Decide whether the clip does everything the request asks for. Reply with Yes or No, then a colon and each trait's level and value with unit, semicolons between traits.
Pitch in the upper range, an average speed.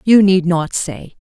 No: medium, 180 Hz; average, 195 wpm